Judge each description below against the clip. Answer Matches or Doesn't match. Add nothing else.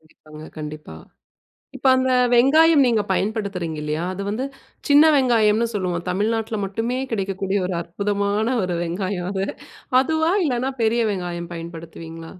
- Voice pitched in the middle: Doesn't match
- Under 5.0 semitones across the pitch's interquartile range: Doesn't match